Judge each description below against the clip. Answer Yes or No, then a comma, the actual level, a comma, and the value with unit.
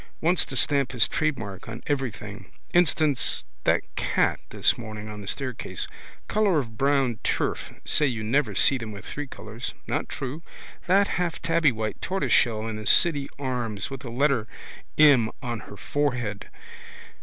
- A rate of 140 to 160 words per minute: Yes, average, 155 wpm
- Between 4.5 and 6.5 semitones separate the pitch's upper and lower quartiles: Yes, average, 4.9 semitones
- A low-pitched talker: Yes, low, 130 Hz